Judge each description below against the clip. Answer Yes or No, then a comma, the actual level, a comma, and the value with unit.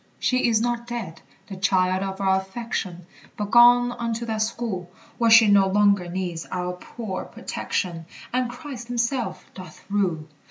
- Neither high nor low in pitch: No, high, 205 Hz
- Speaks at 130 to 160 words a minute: Yes, average, 155 wpm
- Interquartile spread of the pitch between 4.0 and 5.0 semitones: Yes, average, 4.3 semitones